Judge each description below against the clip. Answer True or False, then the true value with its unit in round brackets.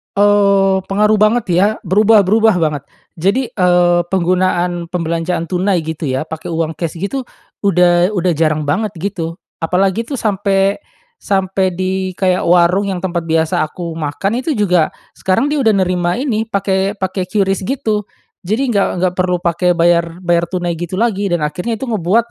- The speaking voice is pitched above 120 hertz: True (185 Hz)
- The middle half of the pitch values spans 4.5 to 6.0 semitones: False (2.9 semitones)